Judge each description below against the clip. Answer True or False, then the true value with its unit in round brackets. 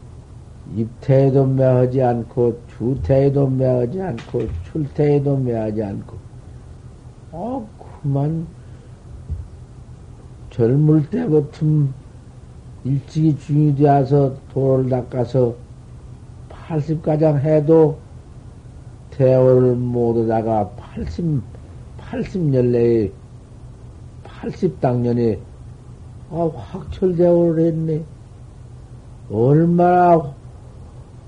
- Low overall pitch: True (125 Hz)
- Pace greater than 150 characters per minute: False (145 characters per minute)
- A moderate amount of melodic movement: True (3.9 semitones)